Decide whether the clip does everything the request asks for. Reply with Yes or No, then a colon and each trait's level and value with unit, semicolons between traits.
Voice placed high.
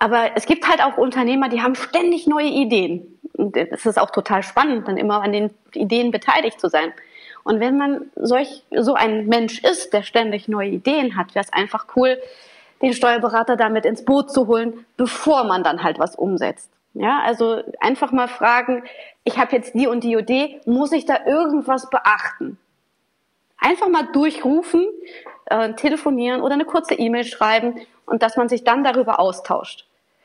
Yes: high, 245 Hz